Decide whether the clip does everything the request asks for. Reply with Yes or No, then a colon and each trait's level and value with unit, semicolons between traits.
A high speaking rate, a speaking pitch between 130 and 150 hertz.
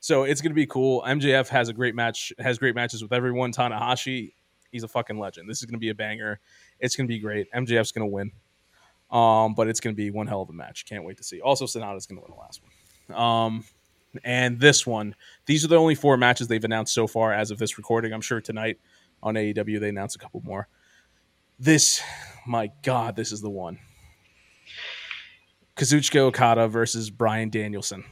No: fast, 215 wpm; low, 115 Hz